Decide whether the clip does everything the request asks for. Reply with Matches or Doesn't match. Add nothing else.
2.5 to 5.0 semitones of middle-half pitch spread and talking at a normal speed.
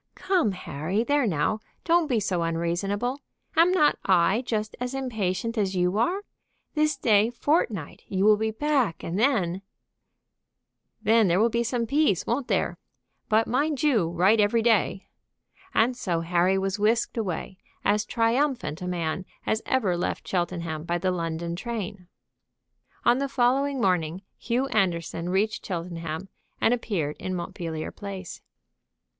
Doesn't match